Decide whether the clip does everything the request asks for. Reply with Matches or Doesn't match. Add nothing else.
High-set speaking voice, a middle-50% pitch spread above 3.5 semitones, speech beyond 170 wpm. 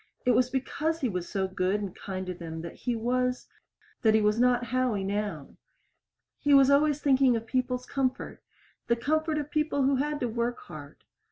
Matches